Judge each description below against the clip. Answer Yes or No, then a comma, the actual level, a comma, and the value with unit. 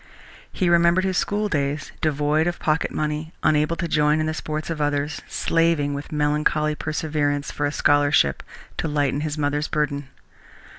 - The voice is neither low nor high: Yes, medium, 150 Hz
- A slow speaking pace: No, average, 155 wpm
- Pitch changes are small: Yes, narrow, 1.4 semitones